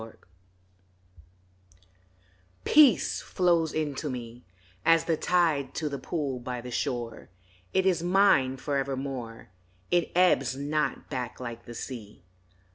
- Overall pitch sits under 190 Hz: Yes, medium, 140 Hz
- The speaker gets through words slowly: Yes, slow, 120 wpm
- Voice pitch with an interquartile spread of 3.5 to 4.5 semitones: No, average, 4.9 semitones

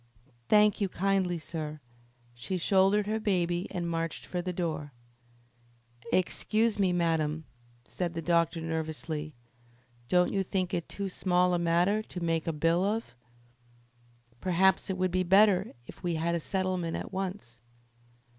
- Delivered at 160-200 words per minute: No, average, 145 wpm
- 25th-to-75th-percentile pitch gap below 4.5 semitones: Yes, narrow, 2.6 semitones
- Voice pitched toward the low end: No, medium, 180 Hz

